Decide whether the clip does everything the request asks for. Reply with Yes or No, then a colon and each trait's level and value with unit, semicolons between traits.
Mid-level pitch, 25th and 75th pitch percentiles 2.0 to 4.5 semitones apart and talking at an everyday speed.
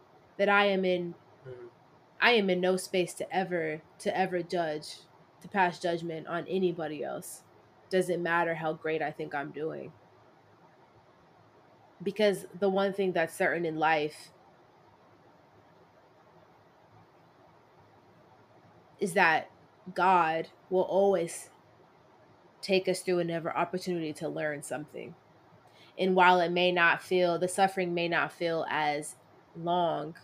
No: medium, 175 Hz; average, 2.7 semitones; slow, 125 wpm